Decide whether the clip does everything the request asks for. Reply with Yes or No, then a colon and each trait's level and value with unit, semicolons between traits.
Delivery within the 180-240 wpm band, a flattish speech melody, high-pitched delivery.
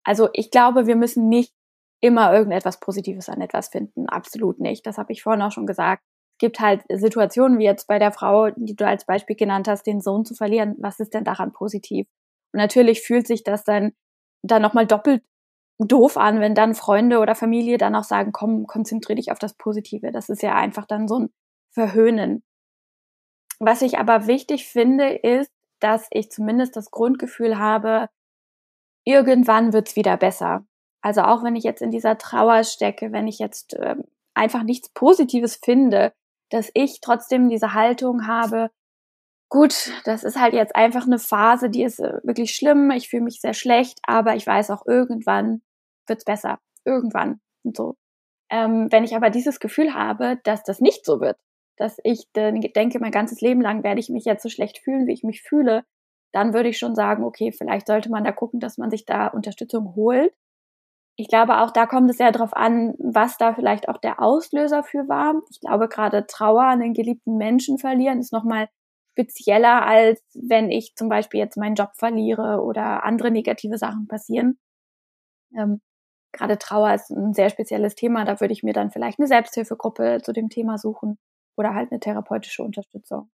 Yes: fast, 190 wpm; narrow, 2.2 semitones; high, 225 Hz